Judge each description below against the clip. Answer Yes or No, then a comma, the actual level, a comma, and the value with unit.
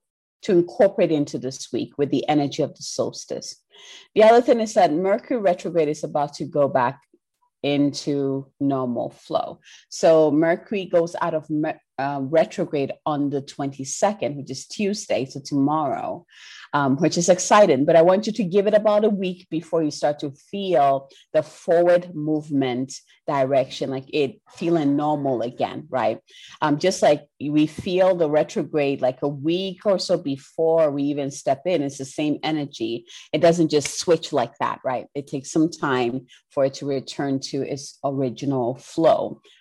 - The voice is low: No, medium, 150 Hz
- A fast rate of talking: No, average, 170 wpm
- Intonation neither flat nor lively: Yes, average, 4.0 semitones